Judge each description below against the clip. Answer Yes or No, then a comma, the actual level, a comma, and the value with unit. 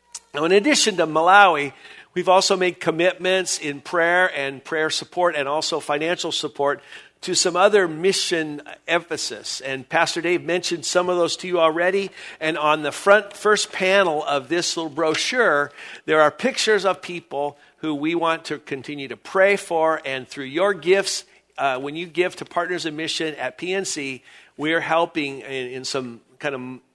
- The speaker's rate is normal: Yes, average, 170 wpm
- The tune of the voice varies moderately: Yes, average, 3.7 semitones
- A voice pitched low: No, medium, 165 Hz